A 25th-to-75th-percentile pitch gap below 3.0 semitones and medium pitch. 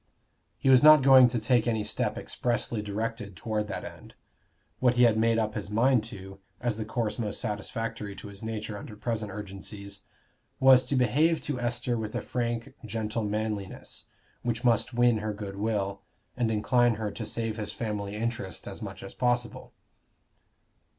No: narrow, 2.5 semitones; low, 110 Hz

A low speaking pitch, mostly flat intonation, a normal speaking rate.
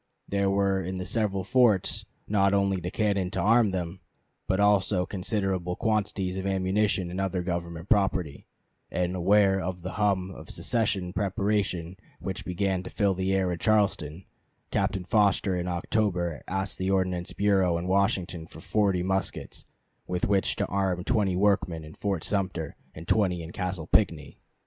Yes: very low, 95 Hz; narrow, 1.9 semitones; average, 160 wpm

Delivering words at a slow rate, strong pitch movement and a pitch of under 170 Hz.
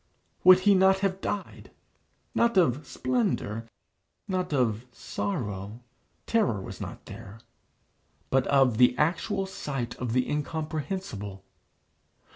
Yes: slow, 110 wpm; wide, 7.9 semitones; medium, 140 Hz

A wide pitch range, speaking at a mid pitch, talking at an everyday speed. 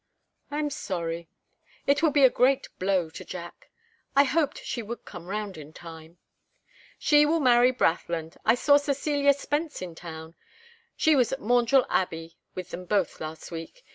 No: wide, 8.8 semitones; high, 220 Hz; average, 170 wpm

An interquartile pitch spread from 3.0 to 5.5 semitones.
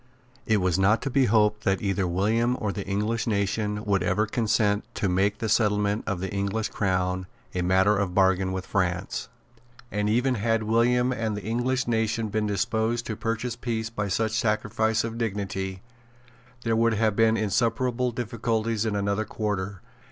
No: narrow, 2.4 semitones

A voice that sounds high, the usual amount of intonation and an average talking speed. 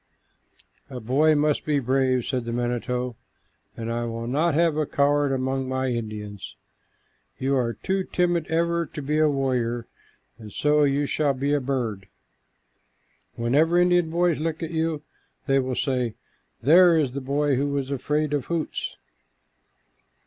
No: medium, 140 Hz; average, 3.7 semitones; average, 155 wpm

